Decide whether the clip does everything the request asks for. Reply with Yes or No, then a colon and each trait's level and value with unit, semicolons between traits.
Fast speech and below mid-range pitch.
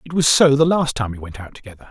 Yes: fast, 315 wpm; low, 130 Hz